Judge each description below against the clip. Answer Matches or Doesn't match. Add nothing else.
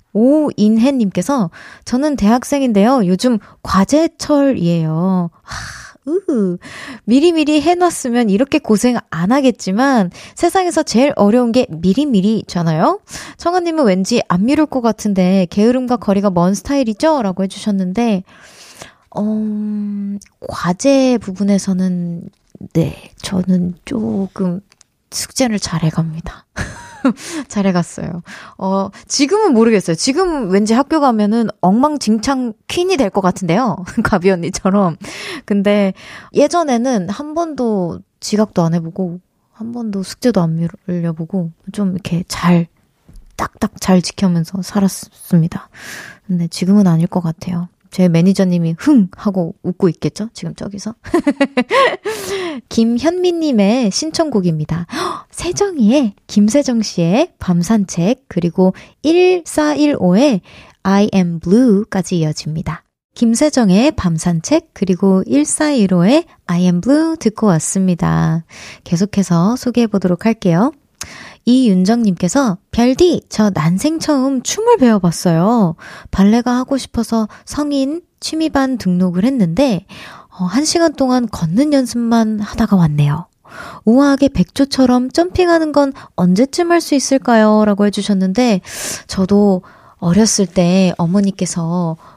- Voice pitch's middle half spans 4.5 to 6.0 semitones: Doesn't match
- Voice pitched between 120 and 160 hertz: Doesn't match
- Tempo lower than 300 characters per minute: Matches